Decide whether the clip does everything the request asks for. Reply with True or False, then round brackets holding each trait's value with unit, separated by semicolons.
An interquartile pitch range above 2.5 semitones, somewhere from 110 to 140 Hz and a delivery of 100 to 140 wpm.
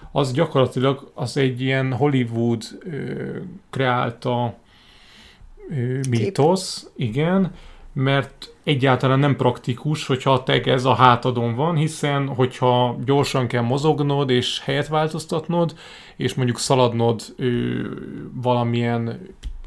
True (2.9 semitones; 130 Hz; 110 wpm)